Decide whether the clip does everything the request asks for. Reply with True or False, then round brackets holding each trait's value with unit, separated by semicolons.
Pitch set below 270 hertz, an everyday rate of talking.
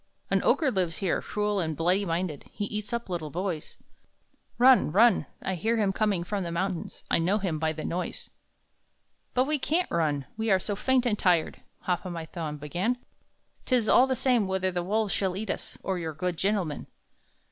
True (190 Hz; 195 wpm)